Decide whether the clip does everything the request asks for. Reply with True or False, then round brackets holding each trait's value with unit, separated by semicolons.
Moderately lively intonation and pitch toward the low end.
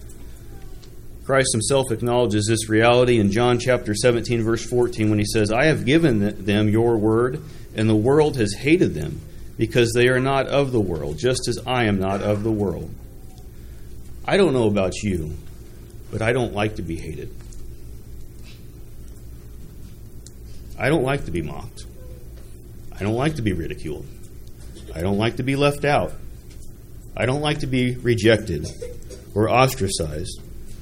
True (3.4 semitones; 110 Hz)